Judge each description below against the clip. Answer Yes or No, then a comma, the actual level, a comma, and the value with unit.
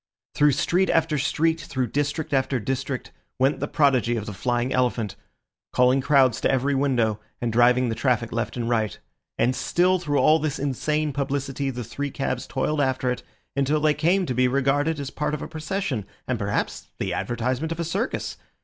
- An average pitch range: Yes, average, 3.4 semitones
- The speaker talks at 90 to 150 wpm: No, average, 185 wpm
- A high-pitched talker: No, low, 135 Hz